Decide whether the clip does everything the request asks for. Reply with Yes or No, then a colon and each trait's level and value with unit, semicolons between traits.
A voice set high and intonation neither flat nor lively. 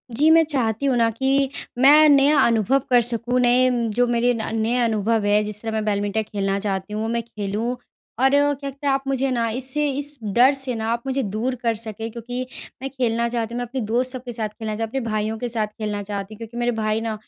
Yes: high, 235 Hz; average, 3.2 semitones